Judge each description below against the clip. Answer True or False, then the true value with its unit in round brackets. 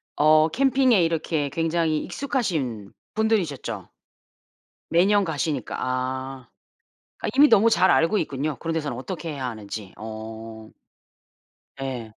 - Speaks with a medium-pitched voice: True (155 Hz)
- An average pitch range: False (6.1 semitones)